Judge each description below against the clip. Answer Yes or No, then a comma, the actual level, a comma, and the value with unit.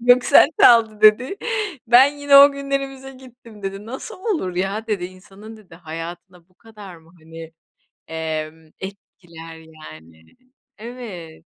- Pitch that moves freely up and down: Yes, wide, 6.8 semitones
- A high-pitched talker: Yes, high, 195 Hz